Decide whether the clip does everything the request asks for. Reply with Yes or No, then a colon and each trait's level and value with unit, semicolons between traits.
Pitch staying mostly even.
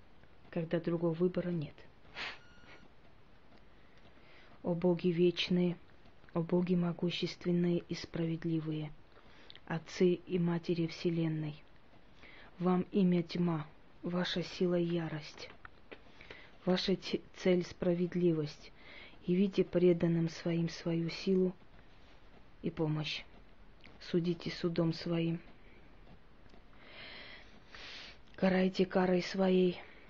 Yes: narrow, 1.4 semitones